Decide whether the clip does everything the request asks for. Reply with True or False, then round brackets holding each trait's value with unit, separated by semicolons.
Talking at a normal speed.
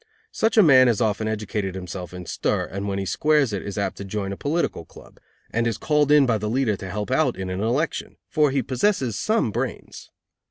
False (225 wpm)